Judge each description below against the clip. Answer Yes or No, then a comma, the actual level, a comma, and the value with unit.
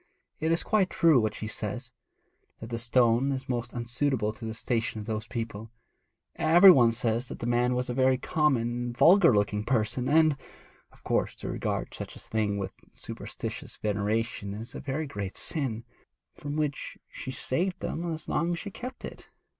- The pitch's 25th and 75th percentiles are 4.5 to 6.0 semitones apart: Yes, average, 5.2 semitones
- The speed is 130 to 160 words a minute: No, average, 185 wpm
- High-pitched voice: No, low, 120 Hz